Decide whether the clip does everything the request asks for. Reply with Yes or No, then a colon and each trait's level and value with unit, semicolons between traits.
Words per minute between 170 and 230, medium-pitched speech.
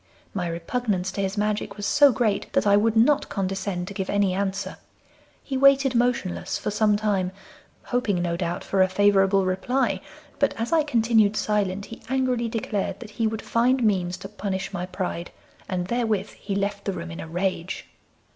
No: average, 185 wpm; high, 205 Hz